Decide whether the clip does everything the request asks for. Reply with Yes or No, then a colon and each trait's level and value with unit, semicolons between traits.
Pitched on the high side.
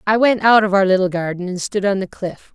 Yes: high, 200 Hz